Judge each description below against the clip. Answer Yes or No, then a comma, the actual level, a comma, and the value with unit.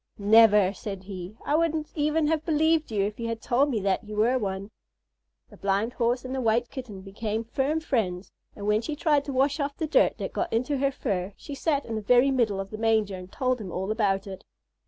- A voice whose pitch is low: No, high, 230 Hz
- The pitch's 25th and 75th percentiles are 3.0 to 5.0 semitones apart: No, wide, 5.5 semitones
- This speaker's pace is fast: Yes, fast, 230 wpm